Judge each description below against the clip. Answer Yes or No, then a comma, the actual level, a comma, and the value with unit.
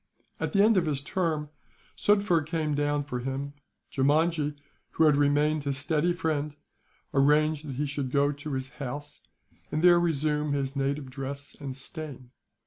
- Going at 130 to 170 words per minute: Yes, average, 160 wpm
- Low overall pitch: No, medium, 145 Hz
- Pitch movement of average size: No, narrow, 2.0 semitones